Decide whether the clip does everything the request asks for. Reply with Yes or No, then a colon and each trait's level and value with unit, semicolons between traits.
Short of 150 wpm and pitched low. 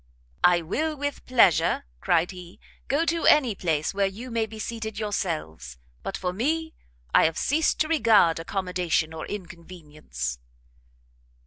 No: average, 140 wpm; high, 195 Hz